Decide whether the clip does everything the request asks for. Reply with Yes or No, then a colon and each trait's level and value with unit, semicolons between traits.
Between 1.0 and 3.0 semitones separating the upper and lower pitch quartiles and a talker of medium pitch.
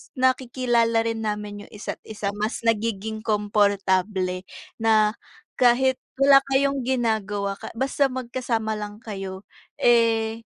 No: average, 2.7 semitones; high, 220 Hz